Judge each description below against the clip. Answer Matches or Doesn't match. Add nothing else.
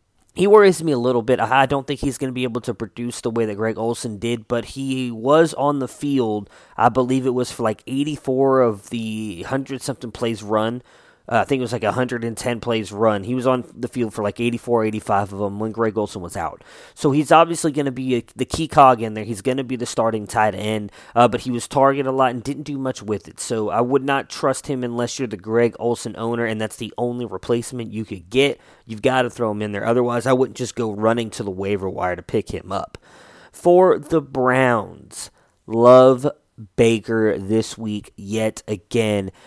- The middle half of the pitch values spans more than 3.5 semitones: Doesn't match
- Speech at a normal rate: Doesn't match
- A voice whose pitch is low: Matches